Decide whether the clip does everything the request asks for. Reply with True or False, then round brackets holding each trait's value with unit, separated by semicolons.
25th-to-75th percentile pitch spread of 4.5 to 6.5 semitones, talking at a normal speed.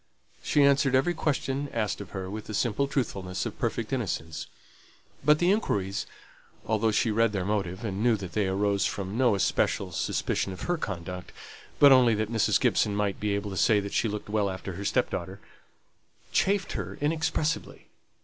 True (5.1 semitones; 180 wpm)